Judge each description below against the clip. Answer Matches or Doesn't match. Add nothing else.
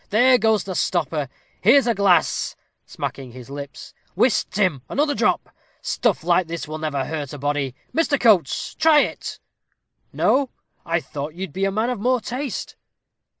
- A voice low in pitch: Doesn't match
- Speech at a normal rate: Matches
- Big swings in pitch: Matches